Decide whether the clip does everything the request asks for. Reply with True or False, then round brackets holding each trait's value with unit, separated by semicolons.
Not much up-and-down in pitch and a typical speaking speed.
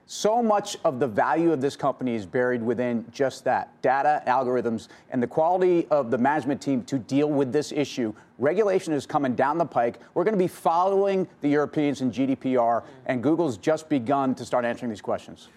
False (4.3 semitones; 195 wpm)